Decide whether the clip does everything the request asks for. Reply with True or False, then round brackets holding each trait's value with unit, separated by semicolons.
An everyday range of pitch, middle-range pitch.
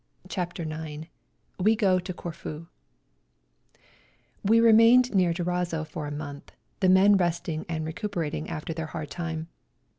True (3.1 semitones; 170 Hz)